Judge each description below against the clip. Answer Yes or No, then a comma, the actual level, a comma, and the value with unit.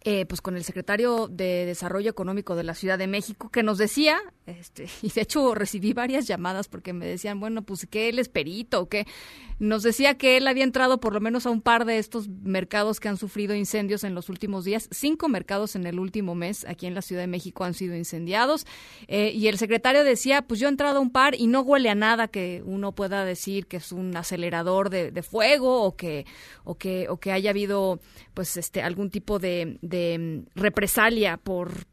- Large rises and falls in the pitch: No, average, 3.8 semitones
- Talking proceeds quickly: Yes, fast, 215 wpm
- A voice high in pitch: Yes, high, 205 Hz